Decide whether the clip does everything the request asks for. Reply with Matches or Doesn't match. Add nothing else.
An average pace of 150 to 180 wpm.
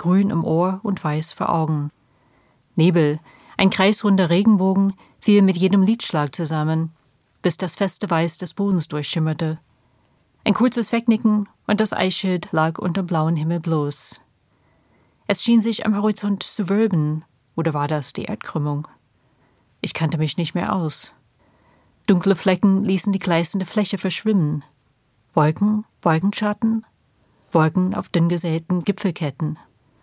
Doesn't match